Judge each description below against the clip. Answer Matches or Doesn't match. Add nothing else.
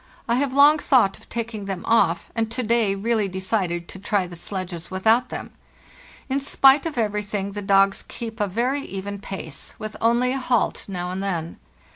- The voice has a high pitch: Matches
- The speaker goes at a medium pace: Matches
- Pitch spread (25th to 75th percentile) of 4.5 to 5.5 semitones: Doesn't match